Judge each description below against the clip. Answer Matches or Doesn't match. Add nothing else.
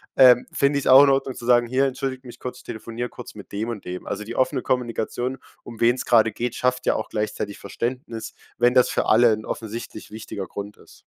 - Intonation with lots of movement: Doesn't match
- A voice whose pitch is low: Matches